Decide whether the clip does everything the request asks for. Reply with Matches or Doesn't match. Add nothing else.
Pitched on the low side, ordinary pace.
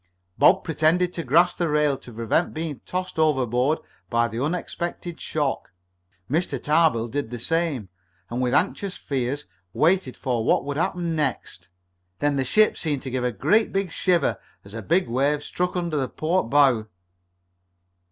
Doesn't match